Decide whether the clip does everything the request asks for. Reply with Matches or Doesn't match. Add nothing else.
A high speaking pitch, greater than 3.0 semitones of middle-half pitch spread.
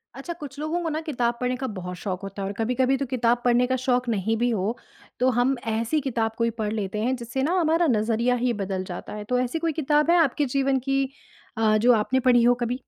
Matches